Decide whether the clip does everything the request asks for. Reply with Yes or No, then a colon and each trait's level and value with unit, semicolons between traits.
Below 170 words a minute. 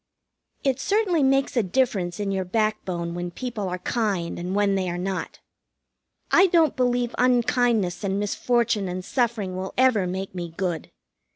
Yes: average, 160 wpm